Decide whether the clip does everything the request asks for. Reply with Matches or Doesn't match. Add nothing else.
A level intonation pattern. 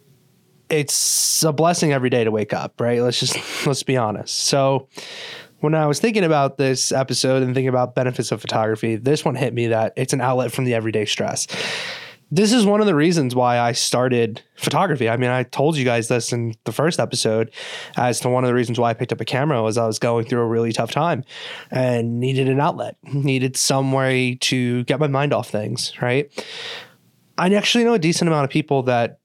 Doesn't match